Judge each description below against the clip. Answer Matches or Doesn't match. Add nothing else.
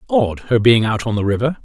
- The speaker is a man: Matches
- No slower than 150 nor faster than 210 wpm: Doesn't match